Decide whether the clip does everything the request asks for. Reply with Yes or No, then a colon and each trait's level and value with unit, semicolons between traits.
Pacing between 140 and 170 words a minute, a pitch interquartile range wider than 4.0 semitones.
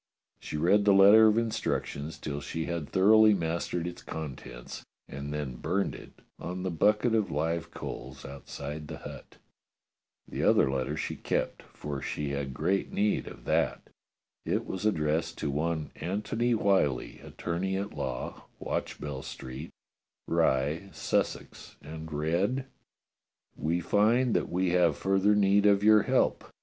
Yes: average, 145 wpm; wide, 5.4 semitones